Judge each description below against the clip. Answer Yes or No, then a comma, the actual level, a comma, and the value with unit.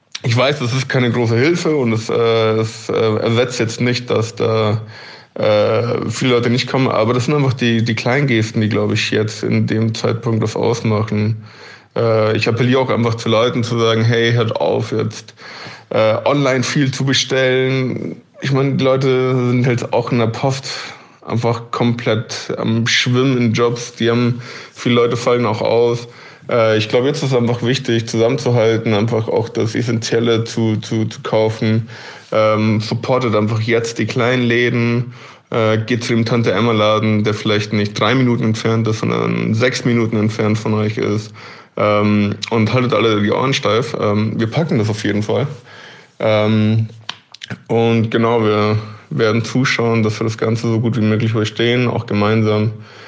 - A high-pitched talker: No, low, 115 Hz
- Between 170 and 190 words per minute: Yes, average, 175 wpm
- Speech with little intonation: Yes, narrow, 1.9 semitones